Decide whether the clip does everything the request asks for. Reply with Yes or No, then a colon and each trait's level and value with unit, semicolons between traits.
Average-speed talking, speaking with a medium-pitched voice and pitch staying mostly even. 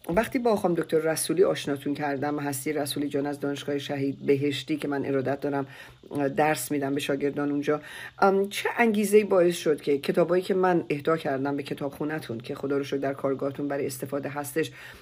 No: fast, 185 wpm; medium, 145 Hz; narrow, 2.1 semitones